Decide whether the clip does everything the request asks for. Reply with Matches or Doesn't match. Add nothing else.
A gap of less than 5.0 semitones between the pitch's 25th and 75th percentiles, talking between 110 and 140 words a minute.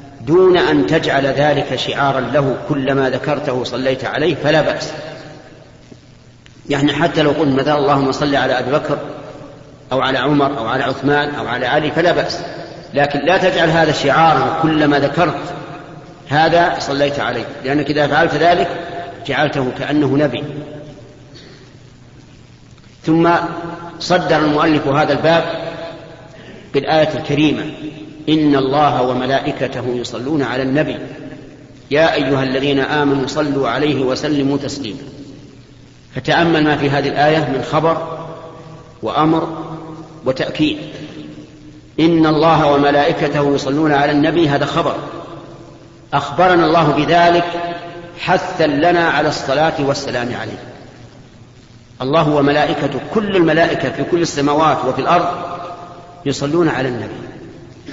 Matches